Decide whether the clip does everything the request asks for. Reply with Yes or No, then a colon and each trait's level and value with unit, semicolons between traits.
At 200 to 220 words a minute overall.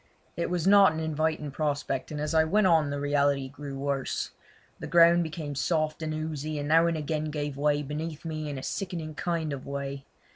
Yes: fast, 205 wpm